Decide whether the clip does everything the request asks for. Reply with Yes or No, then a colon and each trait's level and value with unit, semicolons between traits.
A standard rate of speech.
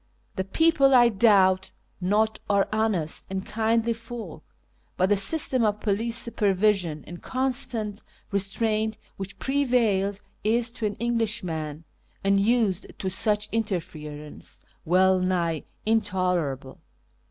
No: slow, 110 wpm